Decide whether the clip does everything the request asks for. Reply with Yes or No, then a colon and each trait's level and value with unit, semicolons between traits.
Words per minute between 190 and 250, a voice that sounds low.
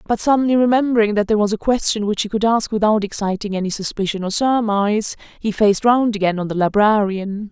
No: average, 200 wpm; high, 210 Hz